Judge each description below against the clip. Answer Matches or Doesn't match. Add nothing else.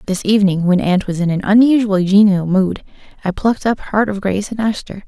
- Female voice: Matches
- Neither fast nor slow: Doesn't match